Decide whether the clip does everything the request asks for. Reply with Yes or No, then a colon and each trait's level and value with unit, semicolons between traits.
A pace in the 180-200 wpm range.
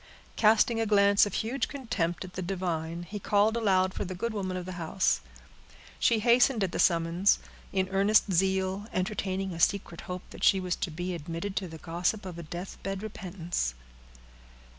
Yes: average, 185 wpm